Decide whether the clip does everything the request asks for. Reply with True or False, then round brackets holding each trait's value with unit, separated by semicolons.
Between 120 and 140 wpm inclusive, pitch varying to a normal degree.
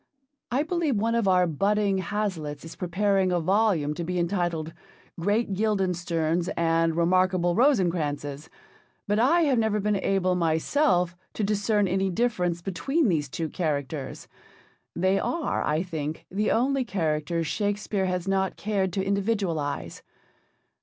True (135 wpm; 3.9 semitones)